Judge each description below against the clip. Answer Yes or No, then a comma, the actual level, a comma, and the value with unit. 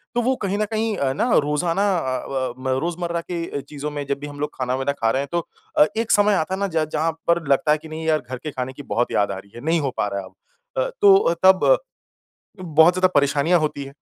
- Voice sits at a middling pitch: Yes, medium, 155 Hz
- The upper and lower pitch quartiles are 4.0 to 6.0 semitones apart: Yes, average, 4.4 semitones